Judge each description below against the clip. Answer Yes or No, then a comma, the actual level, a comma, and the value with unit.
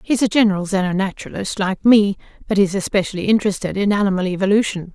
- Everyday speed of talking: Yes, average, 170 wpm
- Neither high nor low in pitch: No, high, 200 Hz